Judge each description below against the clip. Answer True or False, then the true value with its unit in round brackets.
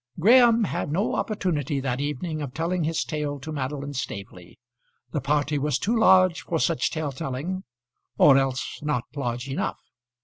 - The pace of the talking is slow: False (160 wpm)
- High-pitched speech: False (150 Hz)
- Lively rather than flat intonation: False (3.7 semitones)